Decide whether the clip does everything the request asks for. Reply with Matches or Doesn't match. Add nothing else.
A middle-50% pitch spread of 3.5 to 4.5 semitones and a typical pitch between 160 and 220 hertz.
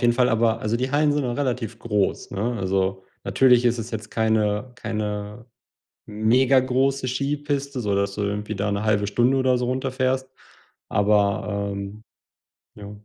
Doesn't match